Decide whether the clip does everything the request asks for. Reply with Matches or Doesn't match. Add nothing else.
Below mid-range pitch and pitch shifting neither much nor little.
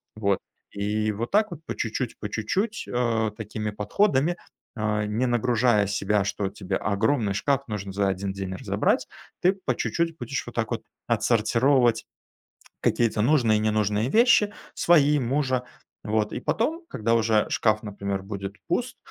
Matches